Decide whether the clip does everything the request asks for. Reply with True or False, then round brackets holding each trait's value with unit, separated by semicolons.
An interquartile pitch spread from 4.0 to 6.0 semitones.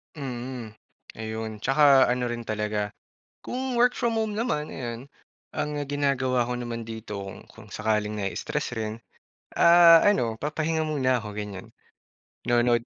True (5.3 semitones)